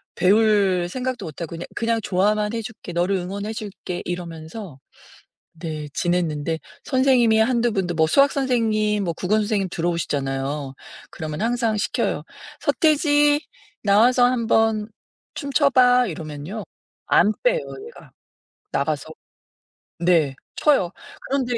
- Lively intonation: Yes, wide, 5.9 semitones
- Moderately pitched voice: No, high, 210 Hz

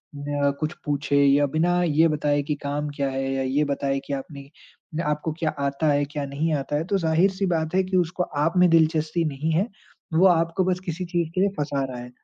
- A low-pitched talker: No, medium, 155 Hz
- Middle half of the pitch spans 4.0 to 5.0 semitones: No, average, 2.9 semitones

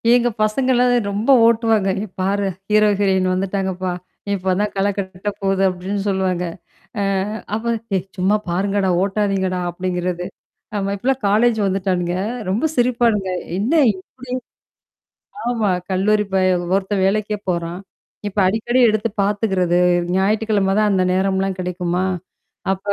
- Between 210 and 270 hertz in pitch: No, high, 195 Hz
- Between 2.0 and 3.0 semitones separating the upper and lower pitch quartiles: Yes, narrow, 2.4 semitones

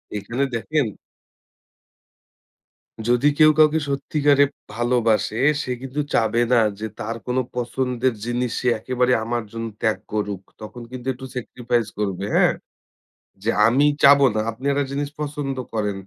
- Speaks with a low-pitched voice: Yes, low, 125 Hz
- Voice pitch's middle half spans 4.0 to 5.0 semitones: No, average, 3.4 semitones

